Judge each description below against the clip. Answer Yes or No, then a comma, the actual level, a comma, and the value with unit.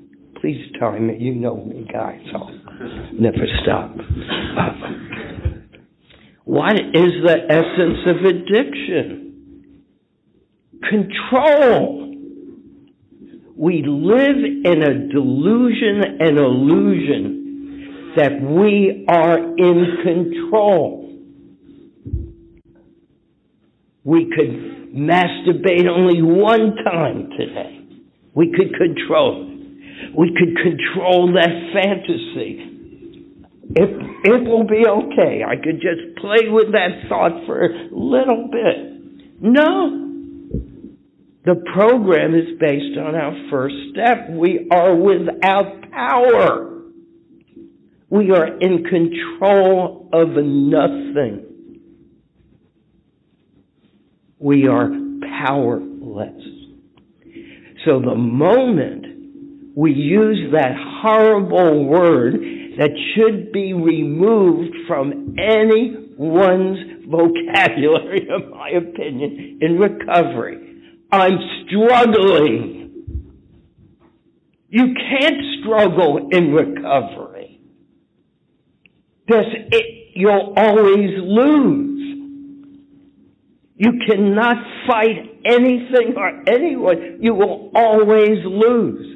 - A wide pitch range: Yes, wide, 8.8 semitones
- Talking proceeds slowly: Yes, slow, 85 wpm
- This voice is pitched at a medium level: No, high, 210 Hz